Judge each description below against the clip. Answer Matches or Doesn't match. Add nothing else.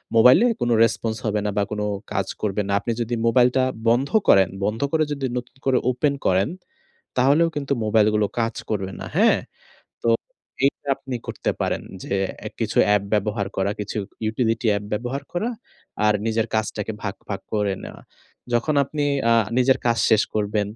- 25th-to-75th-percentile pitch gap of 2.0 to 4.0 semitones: Matches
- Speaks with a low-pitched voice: Matches